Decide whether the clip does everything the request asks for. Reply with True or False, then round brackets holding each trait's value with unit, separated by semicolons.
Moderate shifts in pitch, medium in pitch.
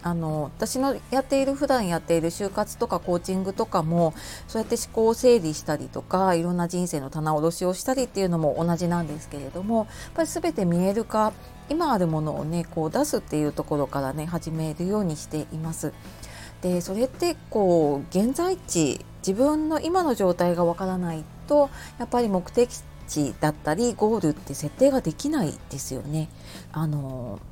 False (6.8 semitones; 175 Hz)